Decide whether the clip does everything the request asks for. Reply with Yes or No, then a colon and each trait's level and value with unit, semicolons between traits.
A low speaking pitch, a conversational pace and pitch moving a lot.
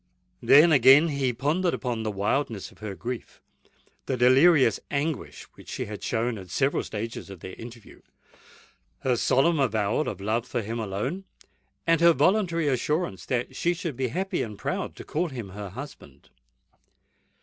Yes: low, 125 Hz; average, 150 wpm; wide, 5.8 semitones